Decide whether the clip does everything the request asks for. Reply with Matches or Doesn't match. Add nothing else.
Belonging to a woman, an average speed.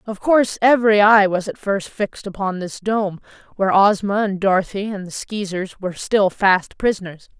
Matches